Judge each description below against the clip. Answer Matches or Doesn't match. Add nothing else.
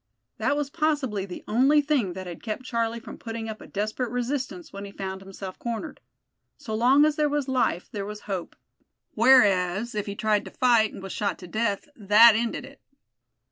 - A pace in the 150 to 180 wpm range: Doesn't match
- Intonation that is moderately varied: Matches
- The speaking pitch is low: Doesn't match